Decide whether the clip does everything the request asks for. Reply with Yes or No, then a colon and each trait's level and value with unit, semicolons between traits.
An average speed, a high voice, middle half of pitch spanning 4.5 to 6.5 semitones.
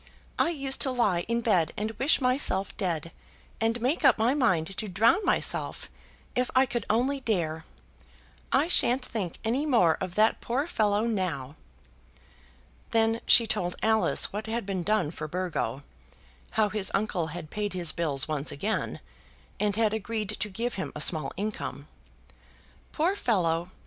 Yes: average, 160 wpm; high, 215 Hz; average, 5.1 semitones